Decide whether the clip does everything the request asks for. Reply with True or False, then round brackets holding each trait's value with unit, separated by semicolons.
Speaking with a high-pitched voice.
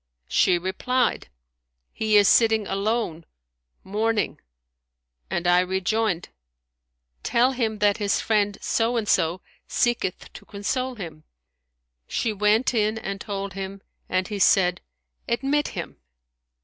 True (210 Hz)